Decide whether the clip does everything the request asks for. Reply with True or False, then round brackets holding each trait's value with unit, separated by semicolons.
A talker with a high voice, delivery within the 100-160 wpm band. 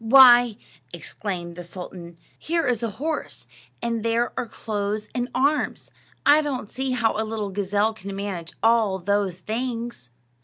True (220 Hz; 150 wpm)